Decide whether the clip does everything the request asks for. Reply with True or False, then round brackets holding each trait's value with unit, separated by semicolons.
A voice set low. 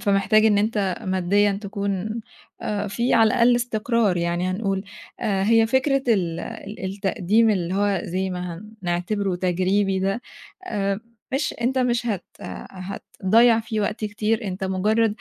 False (205 Hz)